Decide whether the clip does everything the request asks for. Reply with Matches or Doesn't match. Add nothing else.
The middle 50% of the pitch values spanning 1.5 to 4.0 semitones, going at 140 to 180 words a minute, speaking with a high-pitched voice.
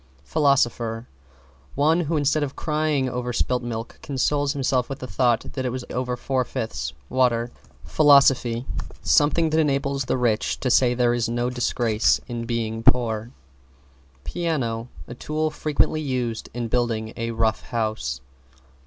Doesn't match